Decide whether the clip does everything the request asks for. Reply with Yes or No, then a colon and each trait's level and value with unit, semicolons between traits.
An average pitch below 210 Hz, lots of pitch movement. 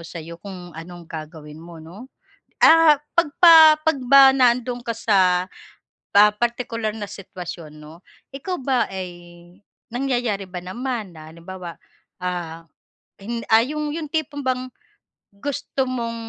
No: high, 215 Hz; wide, 6.7 semitones